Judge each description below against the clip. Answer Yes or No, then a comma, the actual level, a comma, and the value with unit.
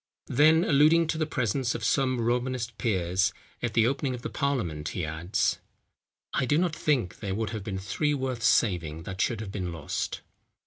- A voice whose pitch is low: Yes, low, 120 Hz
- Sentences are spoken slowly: No, average, 180 wpm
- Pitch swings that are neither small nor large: No, wide, 6.3 semitones